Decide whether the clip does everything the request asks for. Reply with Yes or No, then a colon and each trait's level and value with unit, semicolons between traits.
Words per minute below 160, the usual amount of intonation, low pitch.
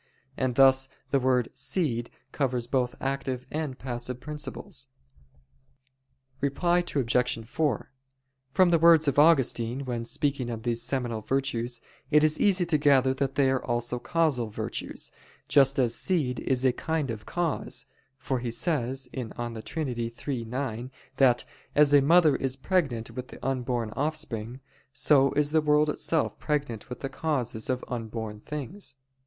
Yes: average, 150 wpm; average, 3.6 semitones; low, 130 Hz